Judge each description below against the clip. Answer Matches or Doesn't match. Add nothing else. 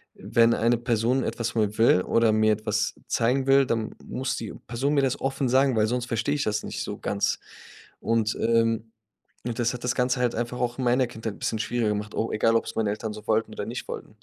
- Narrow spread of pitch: Matches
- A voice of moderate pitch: Doesn't match